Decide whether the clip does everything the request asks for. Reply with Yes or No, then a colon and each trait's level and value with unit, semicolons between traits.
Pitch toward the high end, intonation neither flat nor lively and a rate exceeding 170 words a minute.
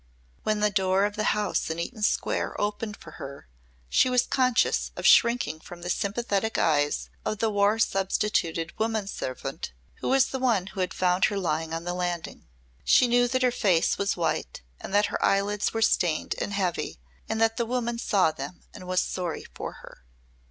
Yes: high, 200 Hz; average, 4.1 semitones; average, 190 wpm